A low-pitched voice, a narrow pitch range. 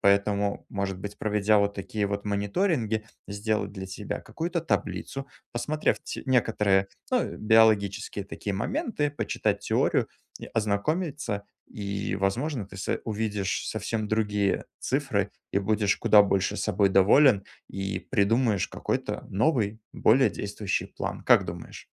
Yes: low, 105 Hz; narrow, 2.3 semitones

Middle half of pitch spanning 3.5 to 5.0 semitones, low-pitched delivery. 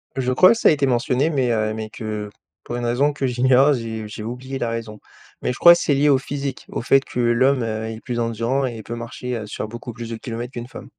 No: average, 2.7 semitones; low, 120 Hz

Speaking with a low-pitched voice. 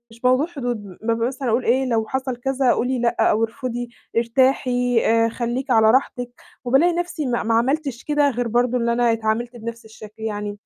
No: high, 240 Hz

